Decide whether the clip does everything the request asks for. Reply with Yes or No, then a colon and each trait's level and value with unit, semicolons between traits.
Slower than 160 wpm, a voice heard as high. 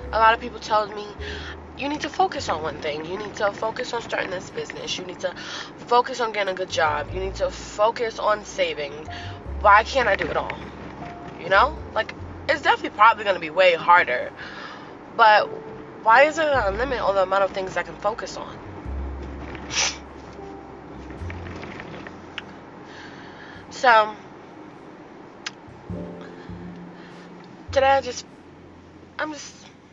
Yes: average, 150 wpm; high, 200 Hz